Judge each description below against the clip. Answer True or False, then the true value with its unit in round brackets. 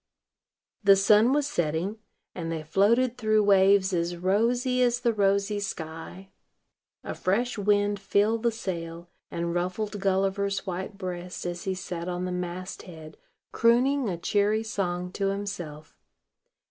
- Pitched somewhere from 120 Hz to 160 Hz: False (195 Hz)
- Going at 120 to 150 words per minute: True (140 wpm)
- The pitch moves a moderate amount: True (3.3 semitones)